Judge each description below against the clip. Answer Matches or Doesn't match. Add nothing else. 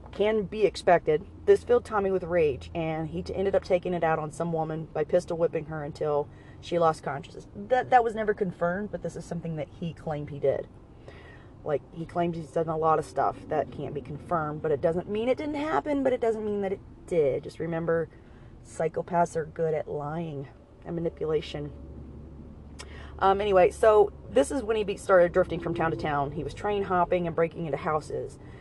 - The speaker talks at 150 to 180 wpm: Doesn't match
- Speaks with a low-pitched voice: Doesn't match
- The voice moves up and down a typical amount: Matches